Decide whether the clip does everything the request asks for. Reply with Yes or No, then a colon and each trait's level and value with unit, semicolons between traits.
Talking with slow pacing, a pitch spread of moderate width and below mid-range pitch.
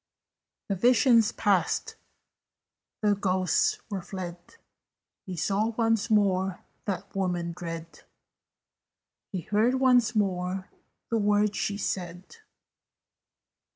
No: slow, 95 wpm; average, 3.0 semitones; high, 195 Hz